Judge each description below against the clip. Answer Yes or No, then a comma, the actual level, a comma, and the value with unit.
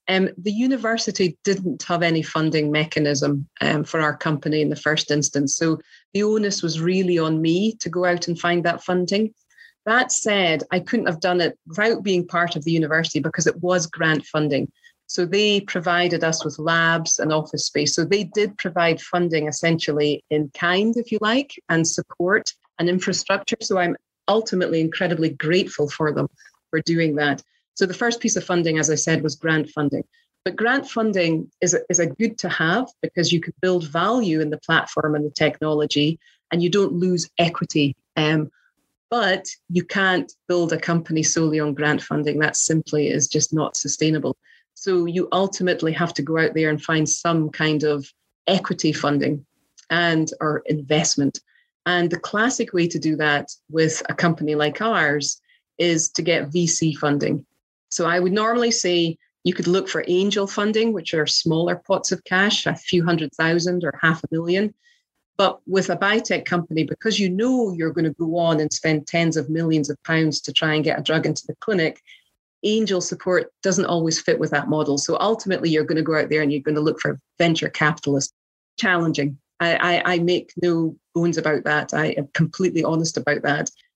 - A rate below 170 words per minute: No, average, 190 wpm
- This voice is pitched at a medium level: Yes, medium, 165 Hz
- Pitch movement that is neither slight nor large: Yes, average, 3.1 semitones